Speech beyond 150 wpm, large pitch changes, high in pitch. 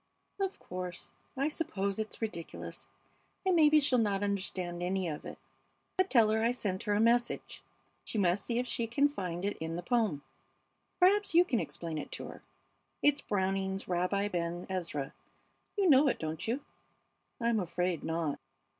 Yes: average, 170 wpm; wide, 5.8 semitones; high, 200 Hz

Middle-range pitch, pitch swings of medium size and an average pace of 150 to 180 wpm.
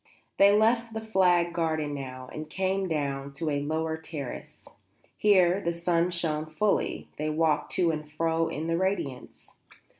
Yes: medium, 165 Hz; average, 3.3 semitones; average, 155 wpm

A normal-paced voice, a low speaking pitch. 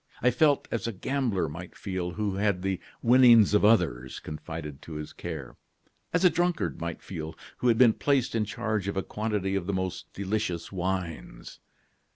Yes: average, 180 wpm; very low, 95 Hz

